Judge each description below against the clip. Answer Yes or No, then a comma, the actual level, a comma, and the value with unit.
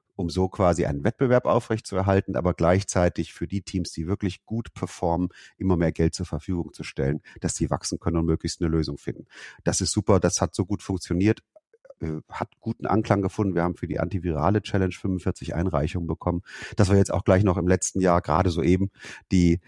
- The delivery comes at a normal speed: No, fast, 195 wpm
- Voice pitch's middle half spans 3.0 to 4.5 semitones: No, narrow, 2.6 semitones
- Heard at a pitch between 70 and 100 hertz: Yes, very low, 90 Hz